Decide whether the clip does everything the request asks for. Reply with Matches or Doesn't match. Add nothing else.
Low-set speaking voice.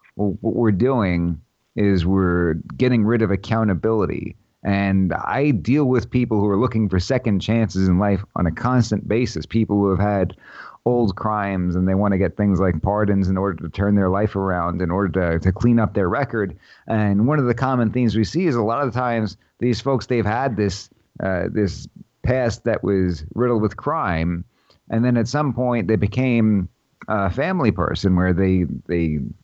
Matches